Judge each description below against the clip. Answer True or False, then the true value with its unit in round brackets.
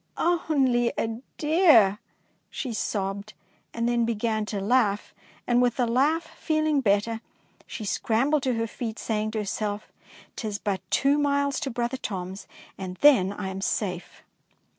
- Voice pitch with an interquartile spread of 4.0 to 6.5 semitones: True (4.6 semitones)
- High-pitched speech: True (230 Hz)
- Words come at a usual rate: True (155 wpm)